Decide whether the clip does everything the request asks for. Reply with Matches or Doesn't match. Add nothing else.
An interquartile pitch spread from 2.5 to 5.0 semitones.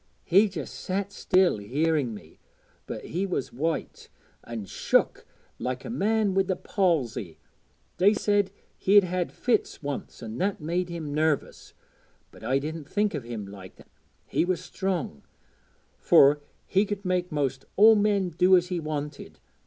Doesn't match